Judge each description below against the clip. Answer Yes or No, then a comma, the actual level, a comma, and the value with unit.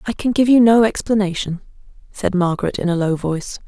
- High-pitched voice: Yes, high, 200 Hz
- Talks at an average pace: Yes, average, 195 wpm